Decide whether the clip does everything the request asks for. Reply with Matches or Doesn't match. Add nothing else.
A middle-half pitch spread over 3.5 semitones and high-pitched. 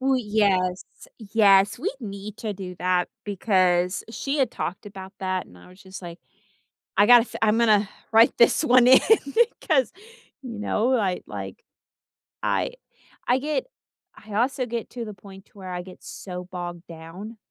Matches